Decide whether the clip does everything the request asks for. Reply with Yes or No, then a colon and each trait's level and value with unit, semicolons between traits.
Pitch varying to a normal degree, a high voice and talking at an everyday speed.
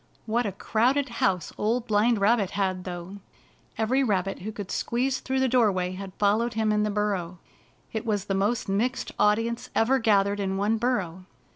Yes: average, 3.2 semitones; high, 210 Hz; average, 175 wpm